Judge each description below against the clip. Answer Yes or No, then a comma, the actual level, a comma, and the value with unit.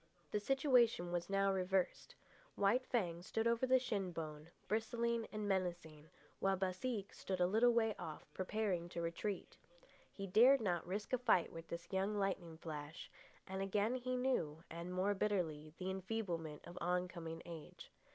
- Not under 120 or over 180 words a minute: Yes, average, 160 wpm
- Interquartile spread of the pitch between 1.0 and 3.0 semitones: No, average, 4.4 semitones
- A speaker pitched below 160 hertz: No, high, 190 Hz